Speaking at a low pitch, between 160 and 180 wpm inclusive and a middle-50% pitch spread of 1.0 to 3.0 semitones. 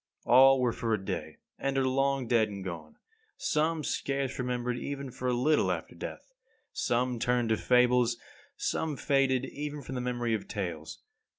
Yes: low, 125 Hz; average, 170 wpm; average, 2.7 semitones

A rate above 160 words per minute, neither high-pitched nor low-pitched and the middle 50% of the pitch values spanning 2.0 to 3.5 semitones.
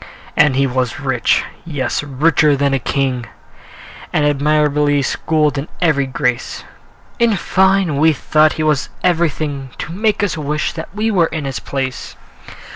No: average, 155 wpm; medium, 150 Hz; average, 2.9 semitones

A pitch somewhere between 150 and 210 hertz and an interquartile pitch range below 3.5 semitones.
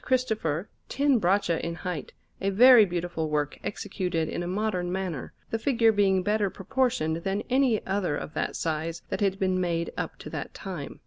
No: high, 190 Hz; average, 4.2 semitones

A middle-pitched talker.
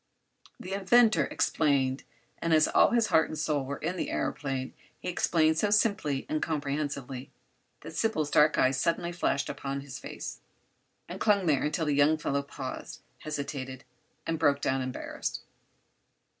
Yes: medium, 150 Hz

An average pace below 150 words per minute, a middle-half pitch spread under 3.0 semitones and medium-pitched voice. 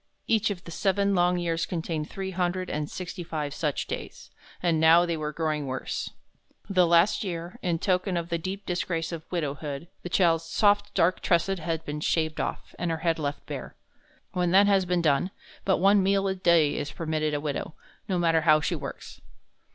No: average, 195 wpm; narrow, 2.6 semitones; medium, 170 Hz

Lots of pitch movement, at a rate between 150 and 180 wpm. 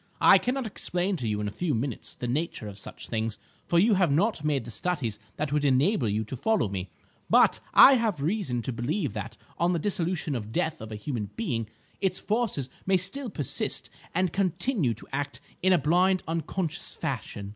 No: wide, 8.2 semitones; average, 200 wpm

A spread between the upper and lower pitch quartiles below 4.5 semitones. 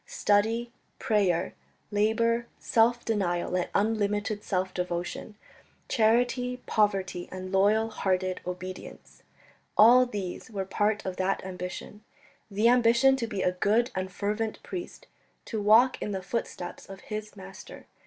Yes: average, 3.2 semitones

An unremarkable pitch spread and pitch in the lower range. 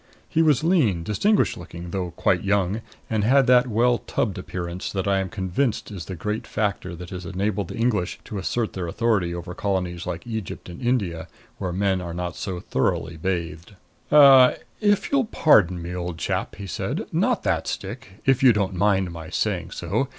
Yes: average, 4.7 semitones; very low, 95 Hz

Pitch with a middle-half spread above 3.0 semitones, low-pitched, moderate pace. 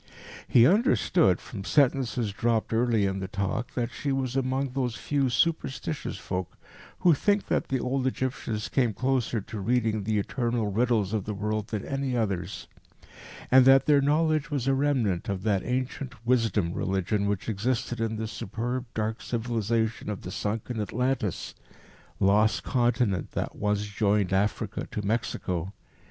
Yes: average, 4.0 semitones; low, 115 Hz; average, 155 wpm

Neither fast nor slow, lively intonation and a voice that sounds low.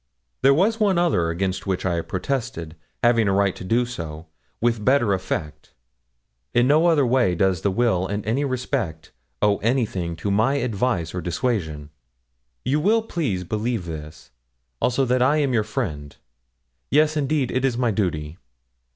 Yes: average, 160 wpm; wide, 6.9 semitones; low, 110 Hz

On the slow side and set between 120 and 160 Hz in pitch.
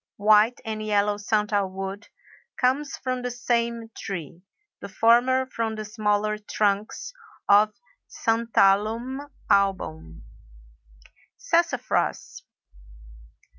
No: slow, 85 wpm; high, 215 Hz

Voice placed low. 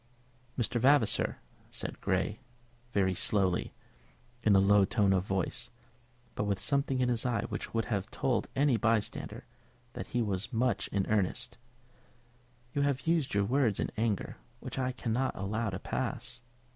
Yes: low, 115 Hz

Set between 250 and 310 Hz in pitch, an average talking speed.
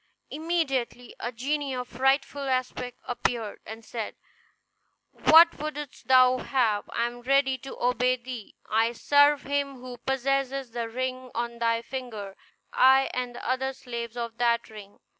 Yes: very high, 255 Hz; average, 145 wpm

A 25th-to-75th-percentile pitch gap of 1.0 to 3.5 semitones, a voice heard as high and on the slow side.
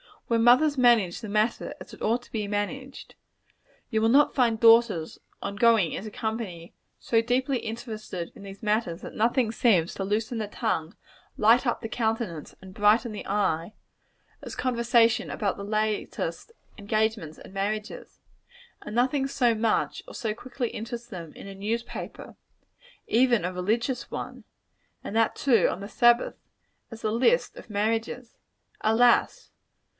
No: narrow, 2.6 semitones; high, 225 Hz; average, 155 wpm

